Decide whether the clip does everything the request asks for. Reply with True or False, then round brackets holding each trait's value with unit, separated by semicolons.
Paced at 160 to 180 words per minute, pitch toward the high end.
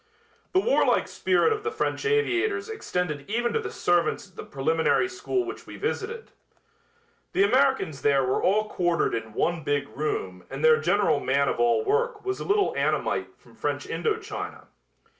True (175 wpm; 210 Hz)